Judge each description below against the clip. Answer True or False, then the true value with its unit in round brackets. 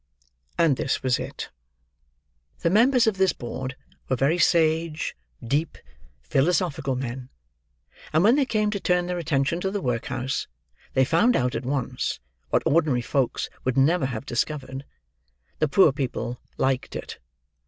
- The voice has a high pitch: False (140 Hz)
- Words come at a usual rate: True (145 wpm)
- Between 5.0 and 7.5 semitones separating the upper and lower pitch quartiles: True (5.3 semitones)